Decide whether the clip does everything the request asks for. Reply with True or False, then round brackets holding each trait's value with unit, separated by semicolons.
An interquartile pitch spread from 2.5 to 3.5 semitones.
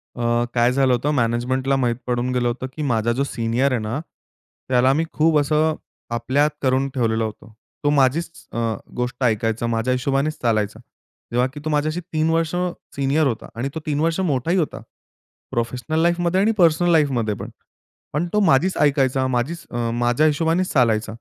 False (4.5 semitones)